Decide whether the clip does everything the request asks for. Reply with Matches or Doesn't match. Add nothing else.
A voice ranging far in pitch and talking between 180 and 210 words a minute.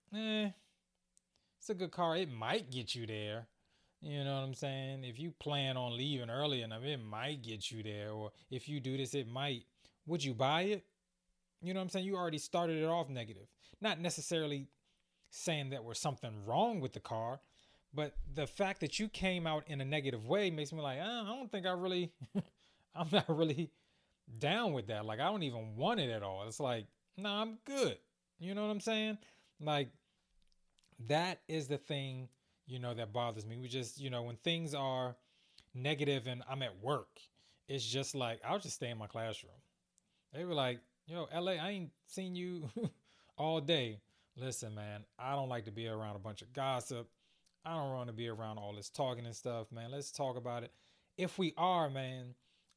Matches